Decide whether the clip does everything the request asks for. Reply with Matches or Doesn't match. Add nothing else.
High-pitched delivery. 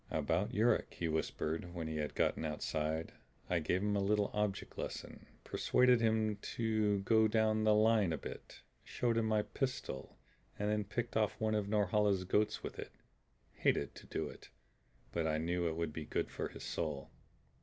Doesn't match